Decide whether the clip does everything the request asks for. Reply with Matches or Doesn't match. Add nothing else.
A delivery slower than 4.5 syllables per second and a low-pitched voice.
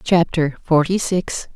Doesn't match